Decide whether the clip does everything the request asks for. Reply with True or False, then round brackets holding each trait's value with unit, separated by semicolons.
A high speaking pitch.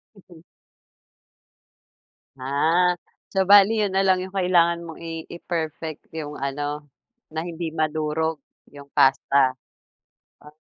False (160 Hz)